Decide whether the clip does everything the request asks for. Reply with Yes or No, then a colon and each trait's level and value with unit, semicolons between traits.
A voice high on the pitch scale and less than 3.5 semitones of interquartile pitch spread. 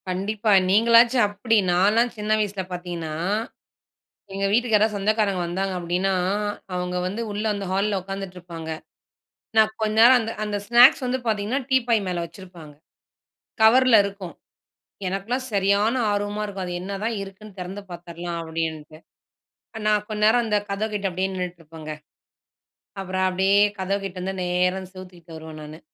Yes: high, 195 Hz; average, 3.1 semitones